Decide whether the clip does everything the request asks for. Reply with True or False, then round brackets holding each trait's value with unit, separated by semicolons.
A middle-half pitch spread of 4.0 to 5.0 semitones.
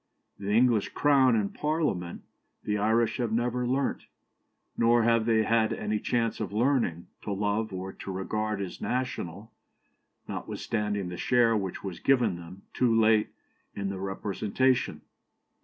False (3.3 semitones)